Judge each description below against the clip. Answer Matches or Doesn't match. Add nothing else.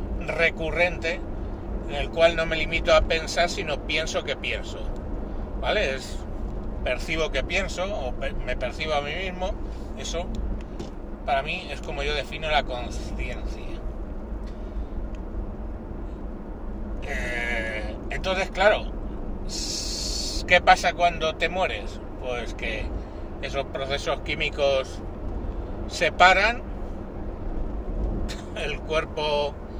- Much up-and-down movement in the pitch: Matches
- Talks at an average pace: Doesn't match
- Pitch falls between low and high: Doesn't match